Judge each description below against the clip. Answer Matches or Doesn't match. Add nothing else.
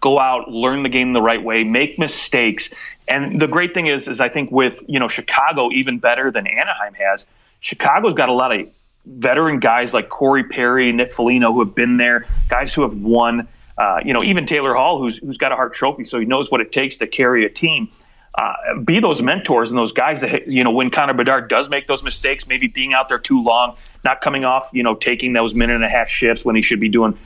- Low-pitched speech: Matches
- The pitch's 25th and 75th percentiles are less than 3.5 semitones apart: Matches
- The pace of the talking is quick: Matches